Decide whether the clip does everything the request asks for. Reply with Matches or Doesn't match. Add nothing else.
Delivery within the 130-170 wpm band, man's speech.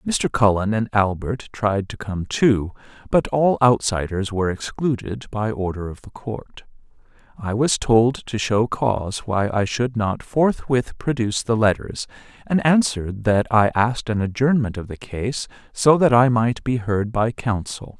Matches